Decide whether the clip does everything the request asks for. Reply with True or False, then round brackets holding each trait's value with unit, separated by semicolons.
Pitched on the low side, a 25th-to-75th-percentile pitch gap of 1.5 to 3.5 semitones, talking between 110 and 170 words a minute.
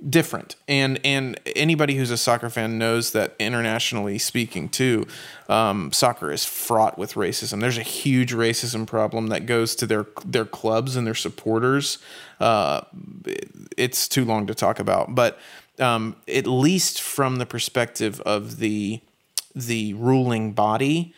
True (120 Hz; 2.9 semitones; 145 wpm)